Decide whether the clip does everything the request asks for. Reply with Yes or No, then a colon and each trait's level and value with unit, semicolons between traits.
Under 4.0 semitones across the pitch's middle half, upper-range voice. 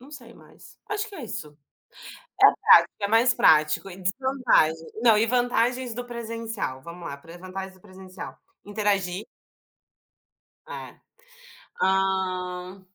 No: average, 4.5 semitones; high, 195 Hz